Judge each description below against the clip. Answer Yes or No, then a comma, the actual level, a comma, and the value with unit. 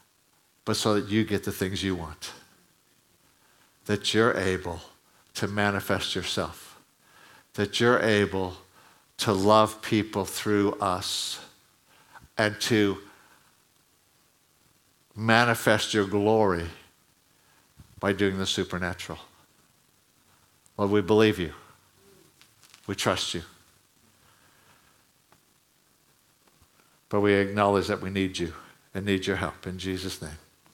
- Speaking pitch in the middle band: No, low, 100 Hz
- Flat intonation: Yes, narrow, 2.3 semitones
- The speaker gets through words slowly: Yes, slow, 100 wpm